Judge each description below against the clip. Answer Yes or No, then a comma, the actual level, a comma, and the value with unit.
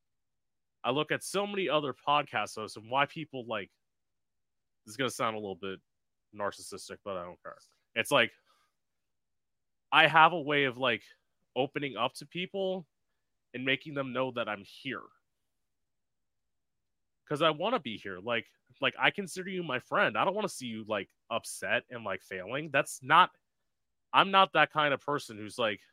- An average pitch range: No, wide, 5.7 semitones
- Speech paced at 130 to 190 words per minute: Yes, average, 180 wpm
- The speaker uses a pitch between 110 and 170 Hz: Yes, medium, 140 Hz